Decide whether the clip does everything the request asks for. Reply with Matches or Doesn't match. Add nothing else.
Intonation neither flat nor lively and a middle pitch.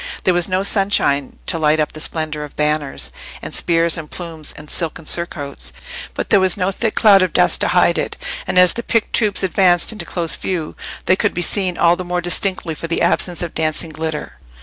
Matches